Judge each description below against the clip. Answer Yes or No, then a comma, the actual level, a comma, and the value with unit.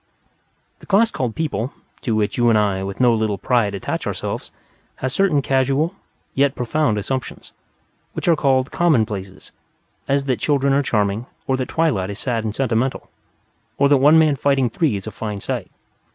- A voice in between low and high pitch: No, low, 130 Hz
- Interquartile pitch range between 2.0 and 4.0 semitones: No, average, 4.5 semitones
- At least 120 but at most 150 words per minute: No, average, 175 wpm